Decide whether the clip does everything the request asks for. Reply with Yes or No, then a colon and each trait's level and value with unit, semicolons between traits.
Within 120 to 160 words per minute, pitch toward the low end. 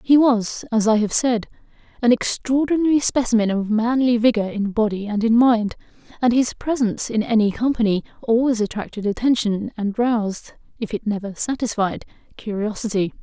No: average, 150 wpm; high, 225 Hz